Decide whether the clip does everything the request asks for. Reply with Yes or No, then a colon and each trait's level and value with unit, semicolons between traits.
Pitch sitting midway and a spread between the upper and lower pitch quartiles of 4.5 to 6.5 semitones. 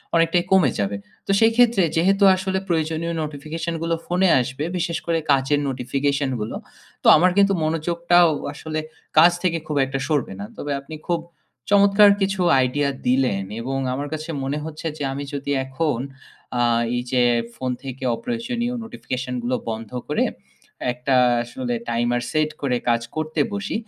Yes: medium, 155 Hz; average, 4.9 semitones